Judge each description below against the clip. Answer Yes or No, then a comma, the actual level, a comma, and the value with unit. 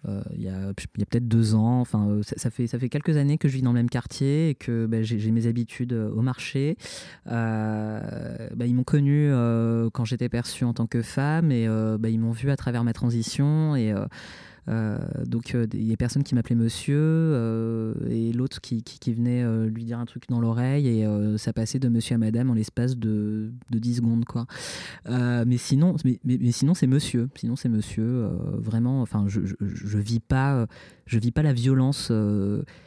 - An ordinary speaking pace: No, fast, 225 wpm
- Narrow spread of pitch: Yes, narrow, 2.2 semitones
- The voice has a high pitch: No, low, 120 Hz